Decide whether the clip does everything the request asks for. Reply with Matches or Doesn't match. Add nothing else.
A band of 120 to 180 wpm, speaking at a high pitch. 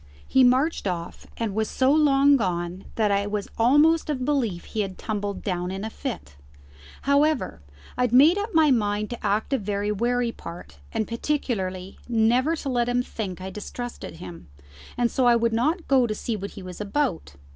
Doesn't match